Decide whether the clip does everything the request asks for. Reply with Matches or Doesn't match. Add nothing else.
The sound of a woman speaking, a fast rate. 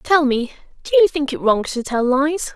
Matches